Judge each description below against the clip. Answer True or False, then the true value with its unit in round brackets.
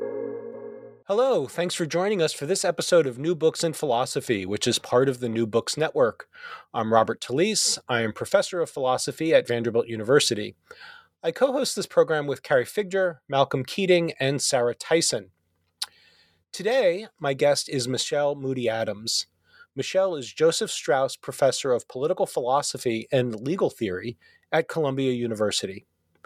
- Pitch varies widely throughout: True (8.3 semitones)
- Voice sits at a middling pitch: True (155 Hz)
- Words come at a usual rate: True (150 wpm)